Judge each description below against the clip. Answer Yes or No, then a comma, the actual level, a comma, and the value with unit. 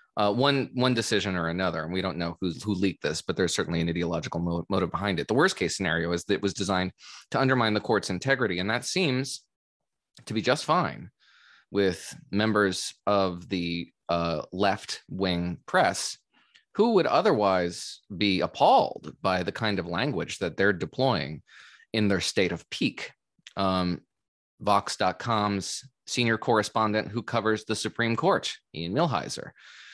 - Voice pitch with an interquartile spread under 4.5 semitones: Yes, average, 4.0 semitones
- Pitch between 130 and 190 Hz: No, low, 100 Hz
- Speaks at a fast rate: No, average, 160 wpm